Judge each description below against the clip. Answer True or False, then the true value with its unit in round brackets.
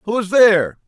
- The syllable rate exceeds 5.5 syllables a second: True (6.0 syllables/s)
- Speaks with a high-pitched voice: True (195 Hz)